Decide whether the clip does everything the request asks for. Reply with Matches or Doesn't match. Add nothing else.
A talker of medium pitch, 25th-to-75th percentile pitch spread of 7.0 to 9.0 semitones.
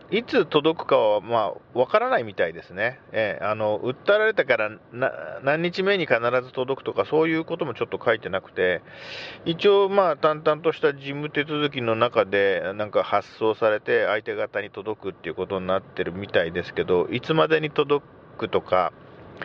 Matches